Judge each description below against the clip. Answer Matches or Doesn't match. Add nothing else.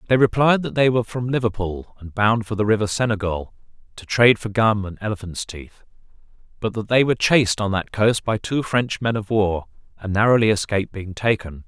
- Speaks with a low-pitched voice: Matches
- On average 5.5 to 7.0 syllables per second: Matches